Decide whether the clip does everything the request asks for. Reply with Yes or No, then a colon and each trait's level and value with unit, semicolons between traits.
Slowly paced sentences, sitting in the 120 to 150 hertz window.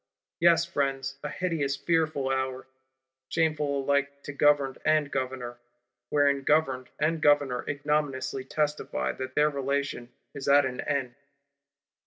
Yes: slow, 125 wpm; medium, 140 Hz